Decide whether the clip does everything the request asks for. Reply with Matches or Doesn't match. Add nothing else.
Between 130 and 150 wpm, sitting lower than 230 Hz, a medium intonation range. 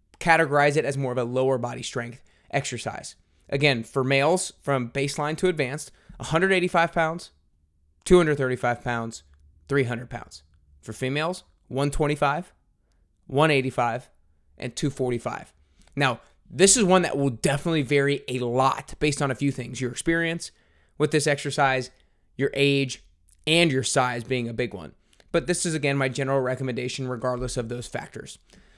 Matches